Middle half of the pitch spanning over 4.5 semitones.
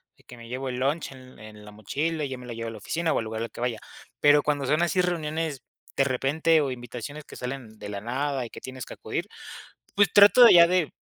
Yes: average, 4.9 semitones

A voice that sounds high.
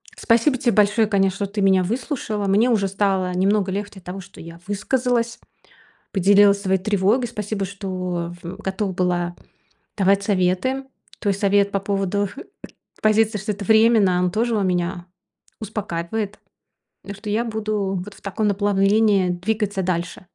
Yes: high, 200 Hz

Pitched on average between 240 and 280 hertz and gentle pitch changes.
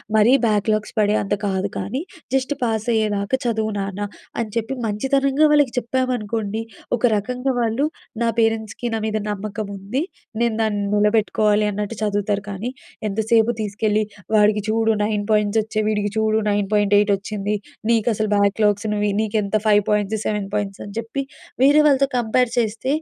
No: high, 215 Hz; narrow, 1.8 semitones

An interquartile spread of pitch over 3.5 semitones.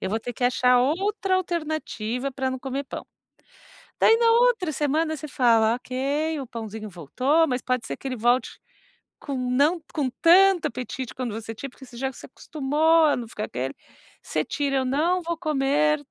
Yes: average, 4.1 semitones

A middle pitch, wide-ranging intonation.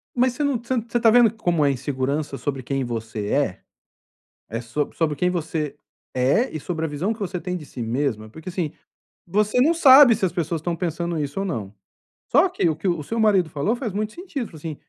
Yes: medium, 170 Hz; wide, 7.5 semitones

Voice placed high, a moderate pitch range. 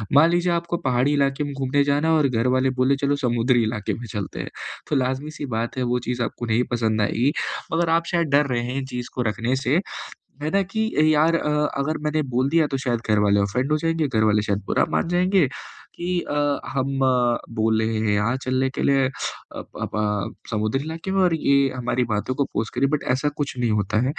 No: low, 130 Hz; average, 4.2 semitones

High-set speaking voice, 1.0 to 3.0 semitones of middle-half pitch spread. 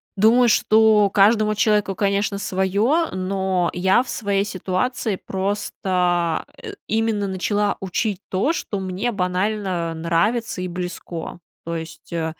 Yes: high, 195 Hz; average, 2.7 semitones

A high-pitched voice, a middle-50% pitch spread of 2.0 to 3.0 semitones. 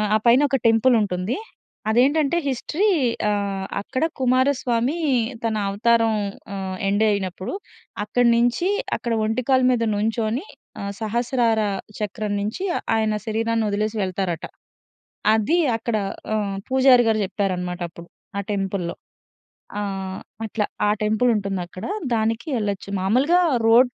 No: high, 220 Hz; average, 3.4 semitones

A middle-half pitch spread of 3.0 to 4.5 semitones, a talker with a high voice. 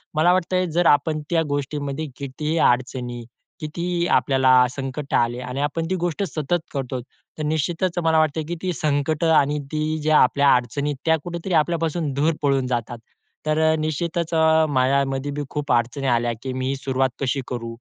No: average, 3.3 semitones; medium, 145 Hz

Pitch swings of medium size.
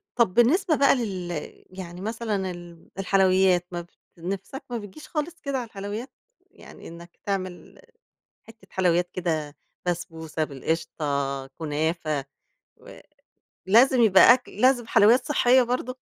No: wide, 5.7 semitones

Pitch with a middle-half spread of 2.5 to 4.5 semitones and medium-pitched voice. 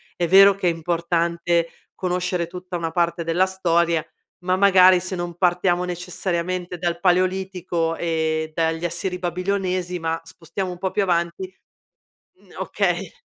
No: narrow, 1.5 semitones; medium, 175 Hz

